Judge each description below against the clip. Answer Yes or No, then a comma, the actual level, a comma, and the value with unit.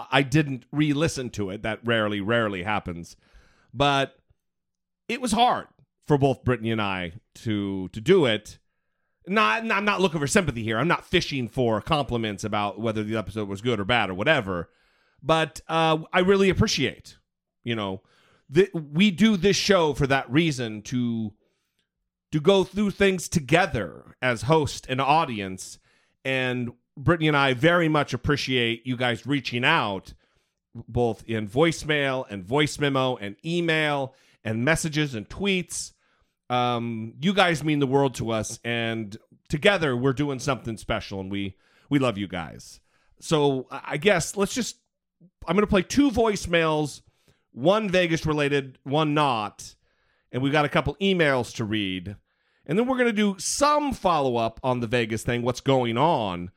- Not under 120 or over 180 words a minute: Yes, average, 160 wpm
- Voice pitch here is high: No, low, 135 Hz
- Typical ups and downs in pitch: No, wide, 6.6 semitones